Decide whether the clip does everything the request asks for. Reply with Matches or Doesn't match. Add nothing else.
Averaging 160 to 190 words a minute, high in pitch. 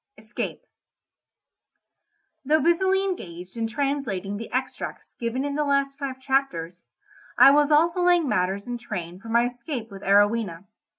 Doesn't match